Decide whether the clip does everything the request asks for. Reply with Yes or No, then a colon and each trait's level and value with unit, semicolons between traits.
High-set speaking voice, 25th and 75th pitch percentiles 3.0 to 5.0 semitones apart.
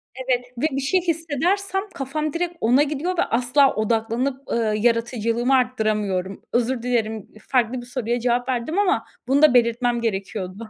Yes: high, 245 Hz; average, 3.4 semitones